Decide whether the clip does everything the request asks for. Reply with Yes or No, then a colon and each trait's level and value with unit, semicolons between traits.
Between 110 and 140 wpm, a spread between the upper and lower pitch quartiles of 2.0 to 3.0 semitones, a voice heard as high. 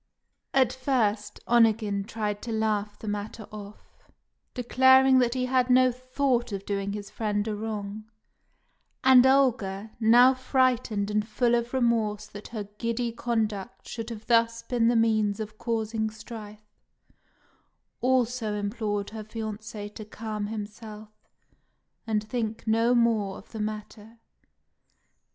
Yes: slow, 135 wpm; narrow, 2.4 semitones; high, 220 Hz